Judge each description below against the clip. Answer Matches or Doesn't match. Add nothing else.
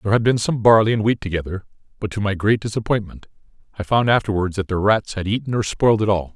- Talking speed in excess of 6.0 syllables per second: Matches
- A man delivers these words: Matches